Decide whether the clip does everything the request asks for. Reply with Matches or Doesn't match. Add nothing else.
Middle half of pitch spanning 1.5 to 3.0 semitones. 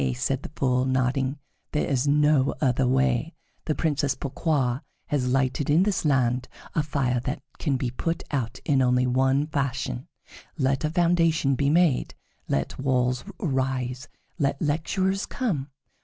Matches